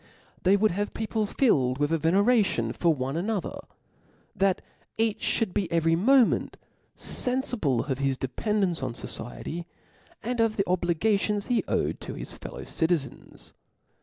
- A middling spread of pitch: No, wide, 5.7 semitones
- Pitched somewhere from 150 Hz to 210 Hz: Yes, medium, 185 Hz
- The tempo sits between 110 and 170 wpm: Yes, average, 140 wpm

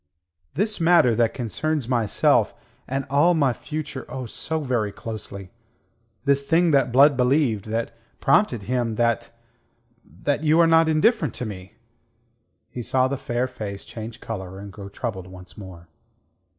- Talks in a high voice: No, low, 125 Hz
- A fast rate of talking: No, average, 150 wpm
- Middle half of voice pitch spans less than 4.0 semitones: No, average, 5.2 semitones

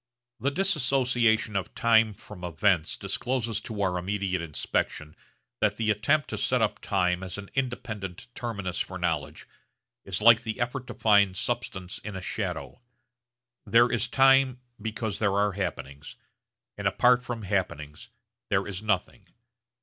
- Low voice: Yes, low, 105 Hz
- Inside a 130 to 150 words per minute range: Yes, average, 145 wpm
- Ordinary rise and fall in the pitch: Yes, average, 4.2 semitones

